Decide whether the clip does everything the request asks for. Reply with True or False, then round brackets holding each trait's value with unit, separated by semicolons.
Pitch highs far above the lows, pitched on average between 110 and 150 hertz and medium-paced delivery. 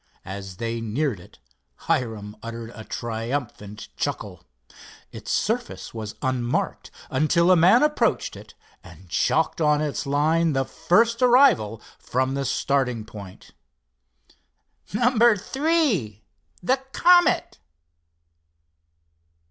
False (8.8 semitones; 135 Hz; 100 wpm)